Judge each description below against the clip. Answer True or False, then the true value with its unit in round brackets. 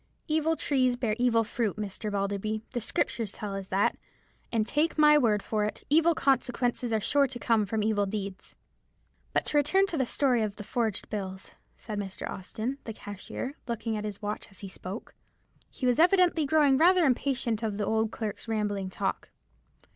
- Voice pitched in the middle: False (225 Hz)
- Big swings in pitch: False (4.5 semitones)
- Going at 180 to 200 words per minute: True (185 wpm)